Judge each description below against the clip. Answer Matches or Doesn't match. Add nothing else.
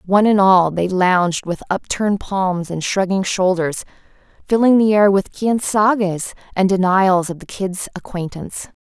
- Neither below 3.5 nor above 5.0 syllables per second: Matches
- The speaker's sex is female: Matches